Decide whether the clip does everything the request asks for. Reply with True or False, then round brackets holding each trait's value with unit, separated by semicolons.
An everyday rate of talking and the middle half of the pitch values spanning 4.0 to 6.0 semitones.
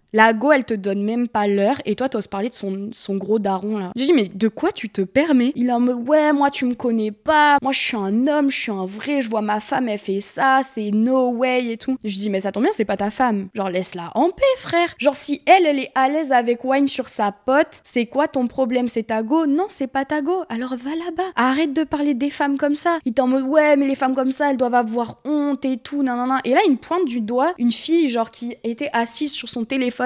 False (280 wpm; 4.6 semitones)